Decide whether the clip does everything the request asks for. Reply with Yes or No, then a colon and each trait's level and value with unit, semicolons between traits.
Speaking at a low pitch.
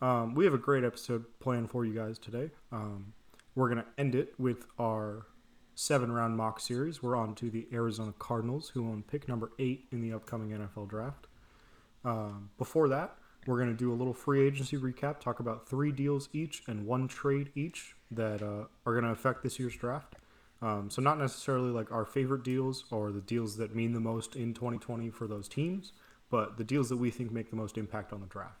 Yes: low, 120 Hz